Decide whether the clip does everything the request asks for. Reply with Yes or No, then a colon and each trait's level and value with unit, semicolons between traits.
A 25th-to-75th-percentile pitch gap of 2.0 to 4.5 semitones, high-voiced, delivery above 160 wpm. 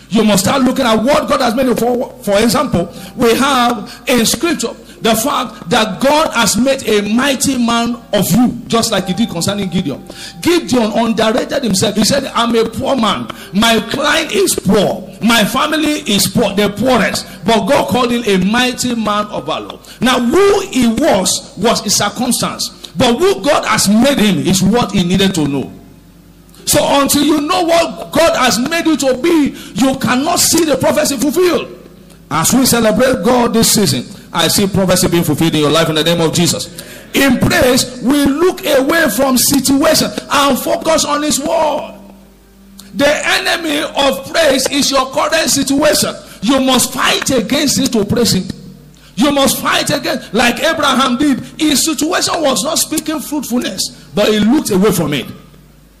No: wide, 5.4 semitones; very high, 250 Hz; average, 175 wpm